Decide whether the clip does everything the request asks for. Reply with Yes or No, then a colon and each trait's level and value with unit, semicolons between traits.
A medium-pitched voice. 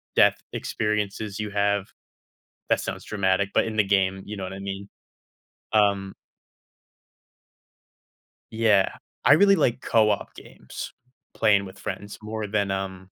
No: low, 100 Hz